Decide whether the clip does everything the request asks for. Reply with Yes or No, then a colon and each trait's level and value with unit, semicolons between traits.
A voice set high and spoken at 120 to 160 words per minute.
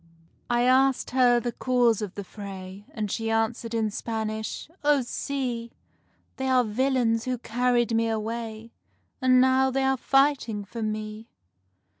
Yes: high, 235 Hz; average, 145 wpm